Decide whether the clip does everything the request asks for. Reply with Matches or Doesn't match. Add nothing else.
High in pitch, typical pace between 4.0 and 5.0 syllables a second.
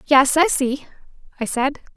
Matches